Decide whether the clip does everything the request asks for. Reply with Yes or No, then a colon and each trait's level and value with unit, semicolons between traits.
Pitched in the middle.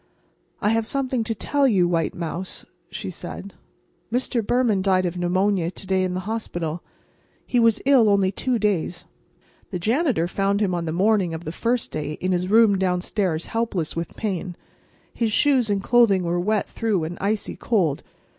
No: high, 195 Hz